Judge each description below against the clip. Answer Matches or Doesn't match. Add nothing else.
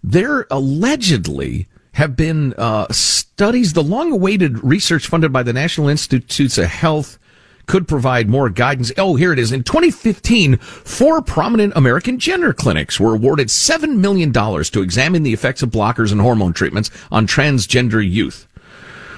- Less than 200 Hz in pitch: Matches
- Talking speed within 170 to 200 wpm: Doesn't match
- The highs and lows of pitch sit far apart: Matches